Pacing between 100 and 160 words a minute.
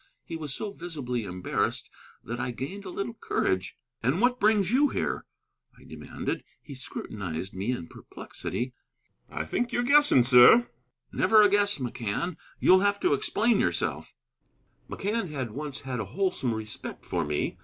Yes: average, 155 wpm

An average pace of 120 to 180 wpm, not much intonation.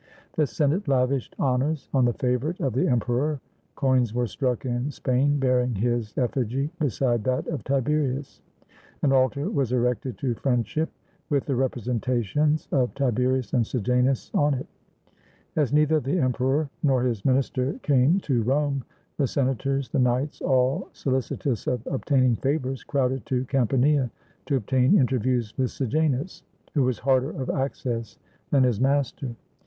Yes: average, 150 wpm; narrow, 2.1 semitones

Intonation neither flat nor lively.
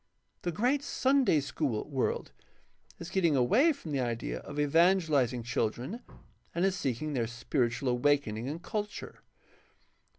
No: wide, 7.4 semitones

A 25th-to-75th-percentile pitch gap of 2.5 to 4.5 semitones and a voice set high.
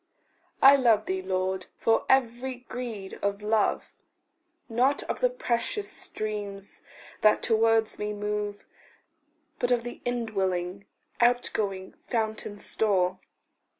Yes: average, 3.3 semitones; high, 215 Hz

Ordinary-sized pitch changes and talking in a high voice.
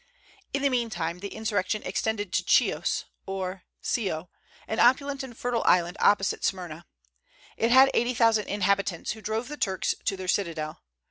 Yes: average, 4.1 semitones; high, 205 Hz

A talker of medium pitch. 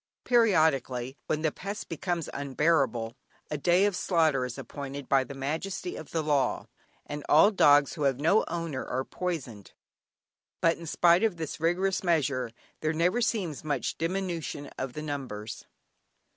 Yes: medium, 155 Hz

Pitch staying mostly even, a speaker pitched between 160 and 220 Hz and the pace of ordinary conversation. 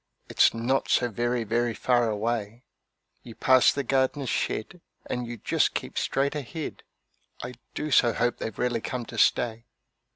No: narrow, 2.2 semitones; low, 120 Hz; average, 160 wpm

